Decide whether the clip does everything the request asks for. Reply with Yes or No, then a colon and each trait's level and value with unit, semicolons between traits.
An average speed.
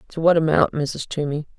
Yes: average, 190 wpm